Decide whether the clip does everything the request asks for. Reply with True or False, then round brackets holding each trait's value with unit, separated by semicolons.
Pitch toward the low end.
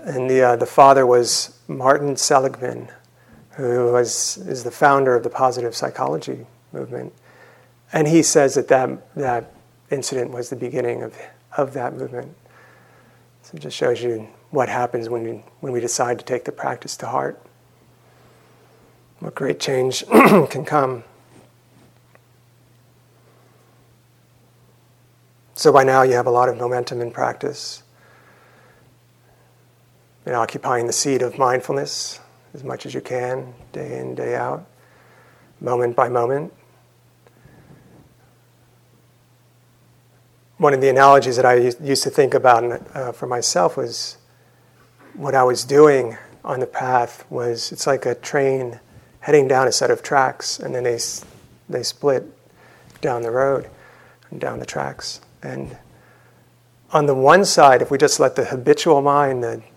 True (125 Hz)